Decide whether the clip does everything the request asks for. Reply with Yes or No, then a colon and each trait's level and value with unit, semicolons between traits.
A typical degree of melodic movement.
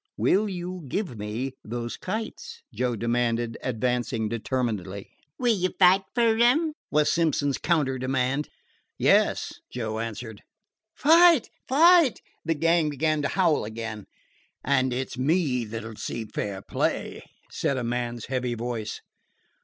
No: wide, 7.4 semitones